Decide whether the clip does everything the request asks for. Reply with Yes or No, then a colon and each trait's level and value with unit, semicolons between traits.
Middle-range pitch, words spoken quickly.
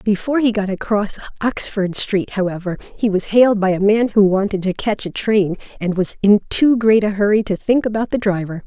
No: high, 205 Hz; fast, 215 wpm